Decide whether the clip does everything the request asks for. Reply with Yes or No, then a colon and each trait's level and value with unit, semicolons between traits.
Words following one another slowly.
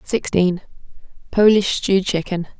Yes: slow, 70 wpm